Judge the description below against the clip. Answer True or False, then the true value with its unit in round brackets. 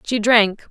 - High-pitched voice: True (220 Hz)